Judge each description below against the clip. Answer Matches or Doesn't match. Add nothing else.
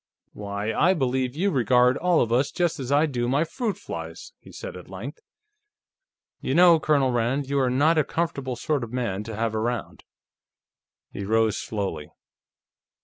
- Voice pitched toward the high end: Doesn't match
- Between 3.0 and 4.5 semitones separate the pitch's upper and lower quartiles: Doesn't match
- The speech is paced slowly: Doesn't match